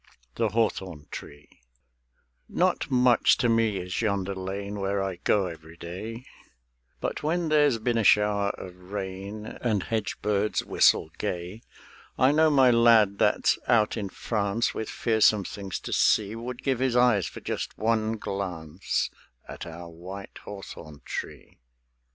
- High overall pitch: No, low, 105 Hz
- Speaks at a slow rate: No, average, 145 wpm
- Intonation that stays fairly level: No, average, 3.4 semitones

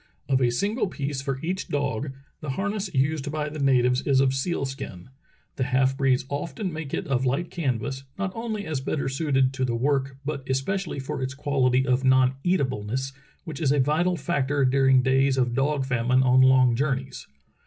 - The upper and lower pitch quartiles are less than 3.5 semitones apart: Yes, narrow, 2.4 semitones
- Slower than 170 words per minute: No, average, 190 wpm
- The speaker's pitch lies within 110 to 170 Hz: Yes, low, 135 Hz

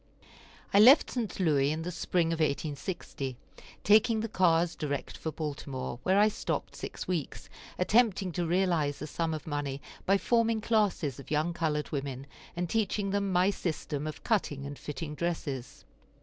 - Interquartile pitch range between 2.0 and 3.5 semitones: No, average, 5.0 semitones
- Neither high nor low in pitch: Yes, medium, 165 Hz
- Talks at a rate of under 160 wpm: No, average, 165 wpm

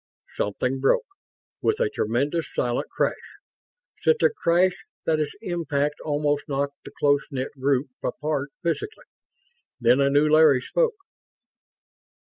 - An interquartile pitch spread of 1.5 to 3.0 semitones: No, average, 3.6 semitones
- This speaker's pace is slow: Yes, slow, 125 wpm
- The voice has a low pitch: No, medium, 145 Hz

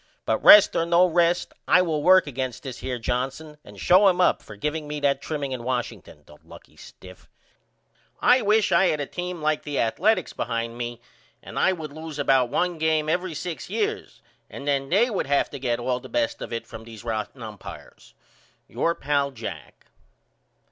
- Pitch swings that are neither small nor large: No, wide, 6.2 semitones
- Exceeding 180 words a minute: Yes, average, 190 wpm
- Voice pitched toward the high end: No, medium, 145 Hz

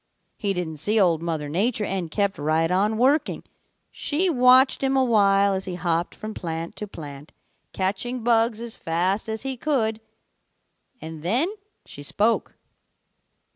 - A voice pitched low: No, high, 200 Hz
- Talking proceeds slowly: No, average, 150 wpm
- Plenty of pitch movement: Yes, wide, 5.7 semitones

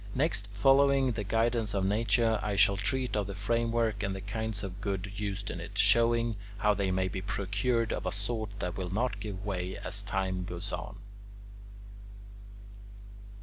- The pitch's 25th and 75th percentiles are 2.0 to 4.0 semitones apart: Yes, average, 2.9 semitones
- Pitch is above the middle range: No, low, 105 Hz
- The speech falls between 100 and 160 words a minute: No, average, 170 wpm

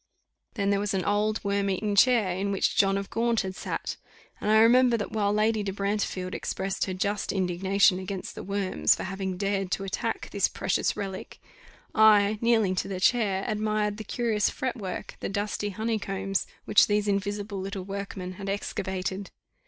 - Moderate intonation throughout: No, narrow, 1.7 semitones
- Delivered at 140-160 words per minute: No, average, 175 wpm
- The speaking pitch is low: No, high, 200 Hz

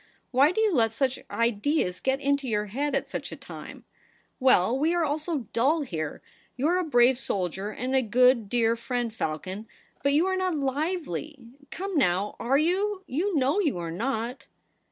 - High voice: Yes, very high, 265 Hz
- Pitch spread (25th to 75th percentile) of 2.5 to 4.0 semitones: No, wide, 5.4 semitones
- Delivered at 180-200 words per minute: Yes, average, 195 wpm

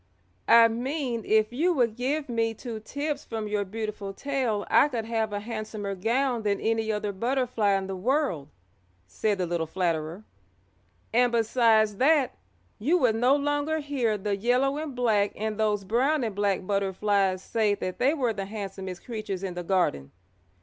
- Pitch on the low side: No, high, 220 Hz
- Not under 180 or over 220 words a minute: No, average, 170 wpm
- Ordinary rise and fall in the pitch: Yes, average, 3.9 semitones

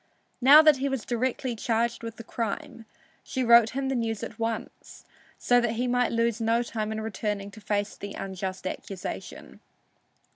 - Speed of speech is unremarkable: Yes, average, 175 wpm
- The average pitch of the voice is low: No, high, 230 Hz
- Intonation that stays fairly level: Yes, narrow, 2.2 semitones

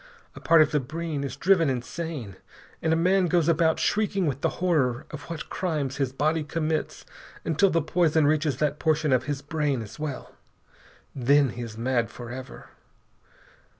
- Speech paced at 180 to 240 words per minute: No, average, 170 wpm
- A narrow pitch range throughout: No, average, 3.6 semitones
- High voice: No, medium, 150 Hz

